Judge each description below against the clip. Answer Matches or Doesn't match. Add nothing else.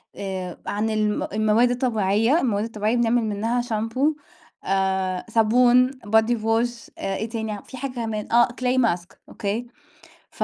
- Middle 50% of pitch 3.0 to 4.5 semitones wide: Doesn't match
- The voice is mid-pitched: Doesn't match